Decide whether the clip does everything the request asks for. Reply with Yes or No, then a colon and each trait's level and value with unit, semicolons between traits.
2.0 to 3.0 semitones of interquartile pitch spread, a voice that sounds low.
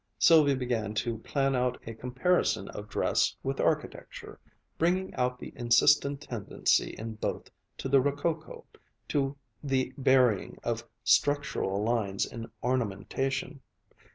No: average, 3.6 semitones; low, 125 Hz